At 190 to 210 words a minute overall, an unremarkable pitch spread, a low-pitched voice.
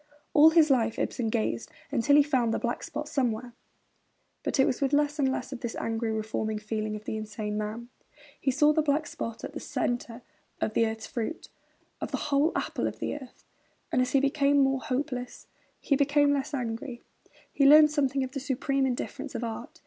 No: average, 200 wpm; average, 4.0 semitones; very high, 260 Hz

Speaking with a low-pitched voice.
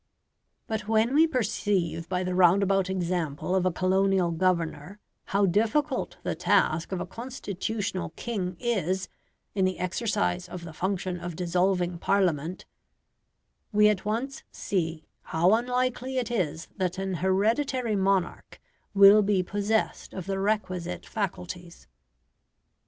No: high, 190 Hz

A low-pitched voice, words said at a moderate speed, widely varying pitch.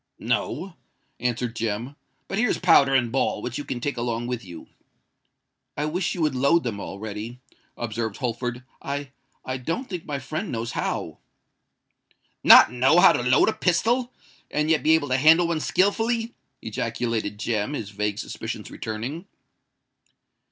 Yes: low, 130 Hz; average, 150 wpm; wide, 5.7 semitones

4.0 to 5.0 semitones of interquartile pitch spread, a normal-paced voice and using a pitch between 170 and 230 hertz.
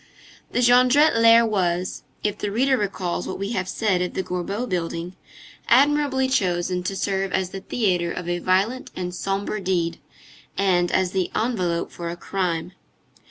Yes: average, 4.3 semitones; average, 160 wpm; high, 190 Hz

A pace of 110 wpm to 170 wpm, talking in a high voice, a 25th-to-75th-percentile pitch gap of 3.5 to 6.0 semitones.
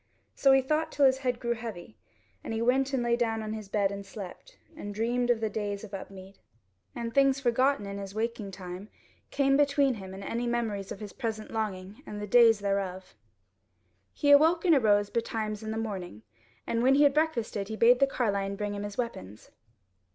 No: average, 200 wpm; high, 225 Hz; average, 3.9 semitones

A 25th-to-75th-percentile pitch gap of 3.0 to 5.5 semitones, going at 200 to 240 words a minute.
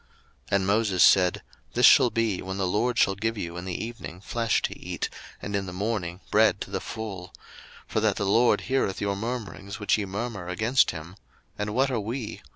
Yes: average, 3.3 semitones; fast, 205 wpm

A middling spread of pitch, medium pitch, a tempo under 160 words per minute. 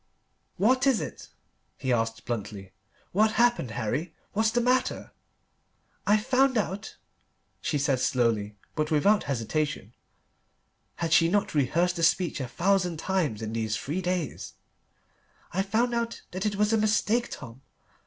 No: wide, 8.6 semitones; medium, 175 Hz; average, 145 wpm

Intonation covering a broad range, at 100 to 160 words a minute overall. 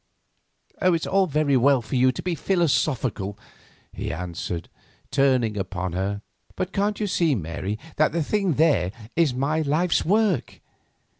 Yes: wide, 8.3 semitones; average, 150 wpm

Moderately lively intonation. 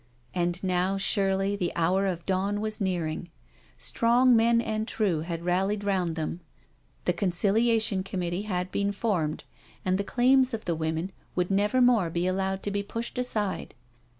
Yes: average, 3.3 semitones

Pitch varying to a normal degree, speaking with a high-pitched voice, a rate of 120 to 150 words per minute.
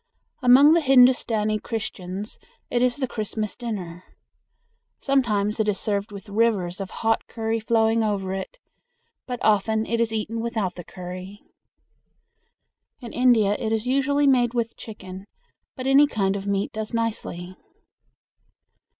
Yes: average, 3.2 semitones; high, 220 Hz; average, 140 wpm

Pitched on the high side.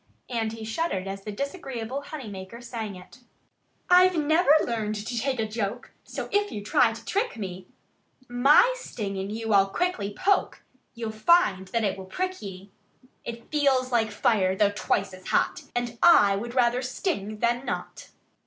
Yes: high, 230 Hz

